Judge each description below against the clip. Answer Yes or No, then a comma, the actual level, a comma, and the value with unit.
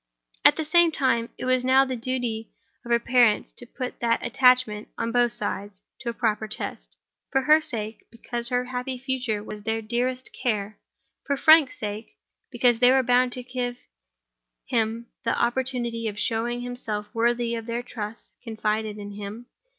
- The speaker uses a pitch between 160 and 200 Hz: No, high, 240 Hz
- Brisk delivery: No, average, 165 wpm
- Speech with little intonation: Yes, narrow, 2.3 semitones